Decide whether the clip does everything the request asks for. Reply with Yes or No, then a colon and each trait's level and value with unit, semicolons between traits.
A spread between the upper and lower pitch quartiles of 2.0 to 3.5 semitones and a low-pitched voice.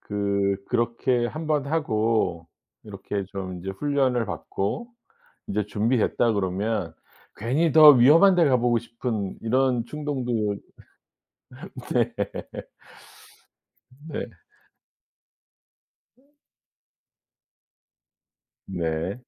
No: average, 5.1 semitones; low, 115 Hz